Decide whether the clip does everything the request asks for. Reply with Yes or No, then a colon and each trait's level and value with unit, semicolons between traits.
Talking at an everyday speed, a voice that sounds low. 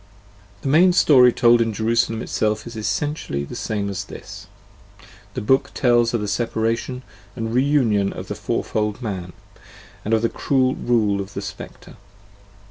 Yes: average, 155 wpm; low, 115 Hz